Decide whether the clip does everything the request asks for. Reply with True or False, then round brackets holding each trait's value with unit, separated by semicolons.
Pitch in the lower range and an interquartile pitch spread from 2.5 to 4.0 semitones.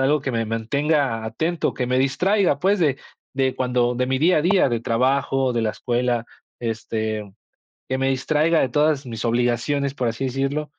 True (130 Hz; 3.5 semitones)